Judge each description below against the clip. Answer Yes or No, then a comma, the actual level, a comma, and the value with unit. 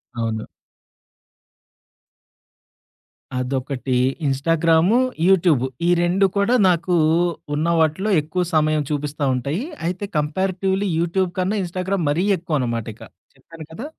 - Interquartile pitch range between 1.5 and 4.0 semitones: No, average, 4.5 semitones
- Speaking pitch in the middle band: Yes, medium, 165 Hz